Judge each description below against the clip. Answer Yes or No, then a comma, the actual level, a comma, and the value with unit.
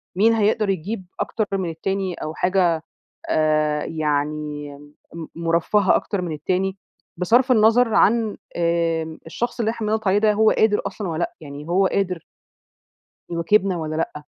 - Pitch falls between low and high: Yes, medium, 180 Hz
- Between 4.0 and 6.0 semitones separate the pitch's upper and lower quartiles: Yes, average, 4.7 semitones